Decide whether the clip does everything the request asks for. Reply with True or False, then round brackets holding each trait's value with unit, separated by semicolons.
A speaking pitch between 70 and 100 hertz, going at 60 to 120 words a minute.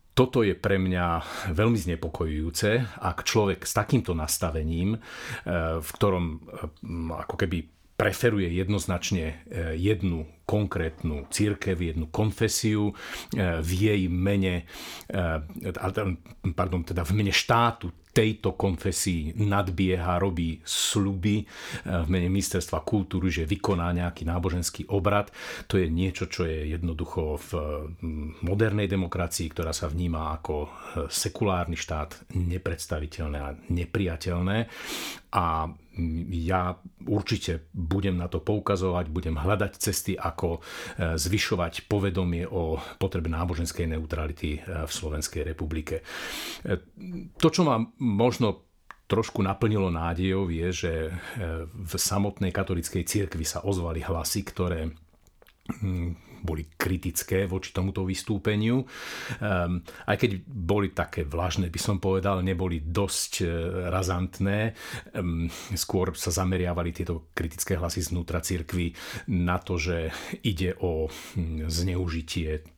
True (90 Hz; 110 wpm)